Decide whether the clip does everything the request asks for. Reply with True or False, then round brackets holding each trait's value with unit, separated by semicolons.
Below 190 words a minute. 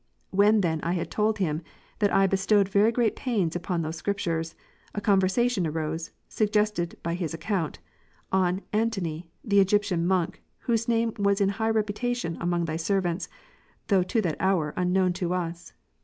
True (165 wpm)